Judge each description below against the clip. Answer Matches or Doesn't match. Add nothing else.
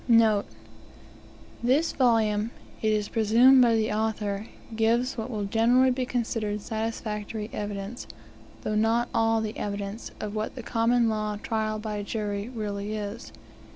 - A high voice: Matches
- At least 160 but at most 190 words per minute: Doesn't match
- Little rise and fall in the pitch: Matches